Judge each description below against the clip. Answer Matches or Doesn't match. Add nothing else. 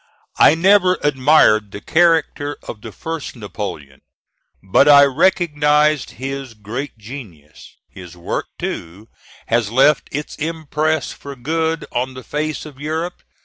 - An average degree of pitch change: Doesn't match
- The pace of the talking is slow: Matches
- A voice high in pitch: Doesn't match